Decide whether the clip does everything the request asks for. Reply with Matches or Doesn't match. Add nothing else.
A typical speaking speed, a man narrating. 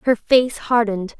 Doesn't match